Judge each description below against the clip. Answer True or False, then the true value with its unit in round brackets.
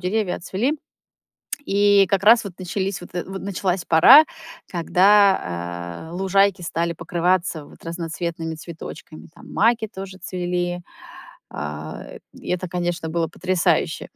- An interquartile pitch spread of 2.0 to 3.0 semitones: True (2.7 semitones)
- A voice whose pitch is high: False (180 Hz)